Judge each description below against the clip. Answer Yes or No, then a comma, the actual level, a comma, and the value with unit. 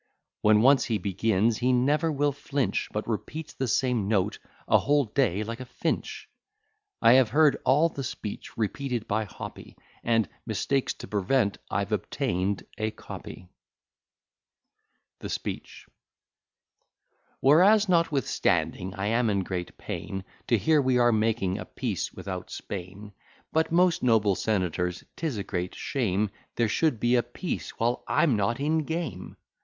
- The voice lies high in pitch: No, low, 115 Hz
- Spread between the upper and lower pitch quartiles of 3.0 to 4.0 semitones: No, wide, 5.4 semitones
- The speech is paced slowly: No, average, 145 wpm